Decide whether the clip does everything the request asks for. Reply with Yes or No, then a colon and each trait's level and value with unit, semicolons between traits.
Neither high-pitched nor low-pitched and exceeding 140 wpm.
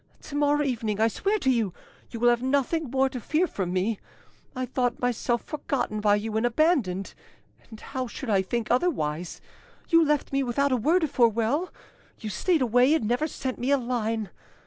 No: high, 245 Hz; average, 190 wpm